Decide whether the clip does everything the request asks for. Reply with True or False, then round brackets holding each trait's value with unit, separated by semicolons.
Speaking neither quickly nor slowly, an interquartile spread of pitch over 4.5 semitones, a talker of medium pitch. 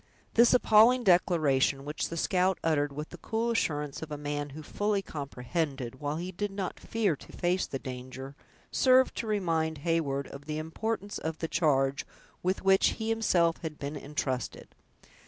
True (170 wpm; 5.2 semitones; 160 Hz)